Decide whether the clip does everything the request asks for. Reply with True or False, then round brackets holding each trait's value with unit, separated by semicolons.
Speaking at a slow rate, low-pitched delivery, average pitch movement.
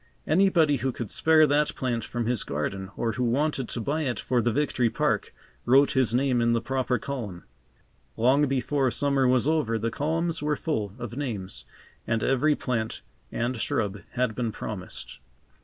False (175 wpm; 125 Hz; 3.9 semitones)